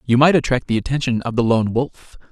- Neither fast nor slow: No, fast, 235 wpm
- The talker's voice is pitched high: No, low, 125 Hz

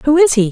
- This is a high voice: Yes, very high, 275 Hz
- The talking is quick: Yes, fast, 345 wpm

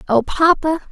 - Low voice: No, very high, 305 Hz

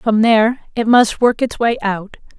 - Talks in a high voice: Yes, high, 225 Hz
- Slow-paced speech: No, average, 200 wpm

